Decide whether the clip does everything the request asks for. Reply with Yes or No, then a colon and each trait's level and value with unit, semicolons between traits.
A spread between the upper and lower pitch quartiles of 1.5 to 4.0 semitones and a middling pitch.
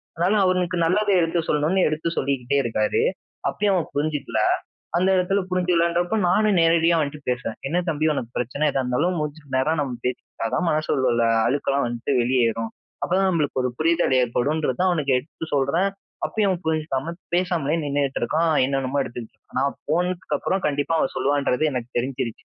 No: average, 4.7 semitones; medium, 150 Hz